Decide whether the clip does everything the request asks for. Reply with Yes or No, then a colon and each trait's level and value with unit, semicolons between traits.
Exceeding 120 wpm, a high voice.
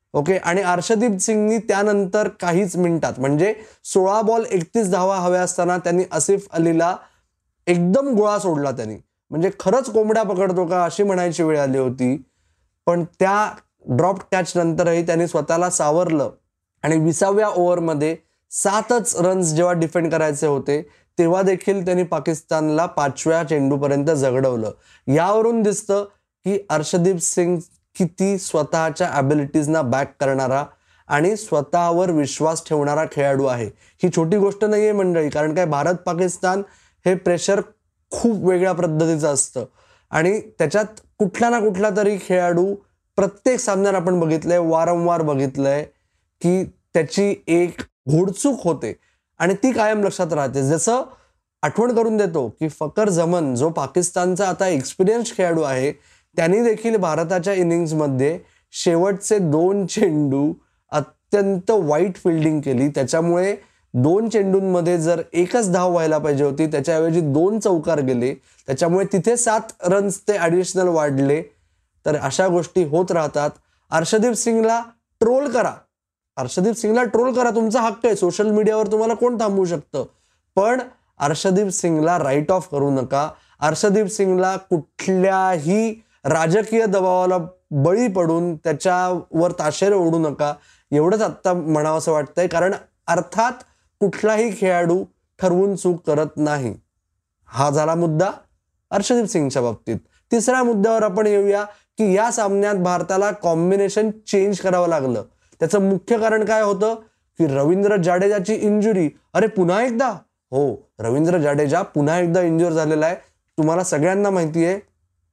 No: fast, 130 wpm; medium, 180 Hz